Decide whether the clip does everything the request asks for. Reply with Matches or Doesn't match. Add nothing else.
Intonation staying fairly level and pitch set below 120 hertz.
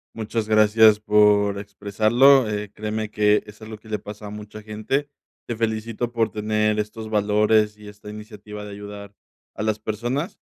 Matches